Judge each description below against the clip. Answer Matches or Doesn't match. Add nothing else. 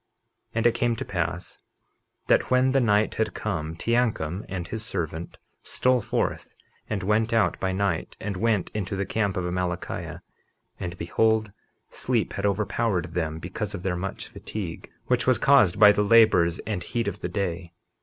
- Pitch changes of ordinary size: Matches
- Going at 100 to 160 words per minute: Doesn't match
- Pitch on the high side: Doesn't match